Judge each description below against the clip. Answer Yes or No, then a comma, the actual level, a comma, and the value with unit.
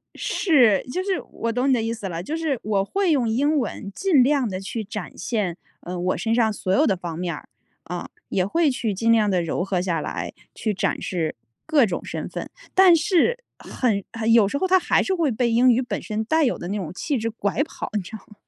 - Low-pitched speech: No, high, 225 Hz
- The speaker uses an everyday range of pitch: No, wide, 6.5 semitones